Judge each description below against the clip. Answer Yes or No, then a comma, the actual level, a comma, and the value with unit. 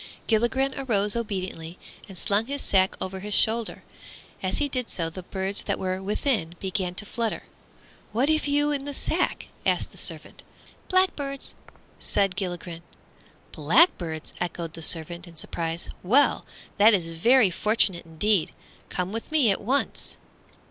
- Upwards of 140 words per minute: Yes, average, 150 wpm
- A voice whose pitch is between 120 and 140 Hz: No, high, 200 Hz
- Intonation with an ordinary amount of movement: No, wide, 6.1 semitones